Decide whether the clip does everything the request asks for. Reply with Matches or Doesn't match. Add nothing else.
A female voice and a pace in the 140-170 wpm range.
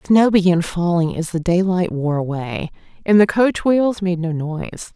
Doesn't match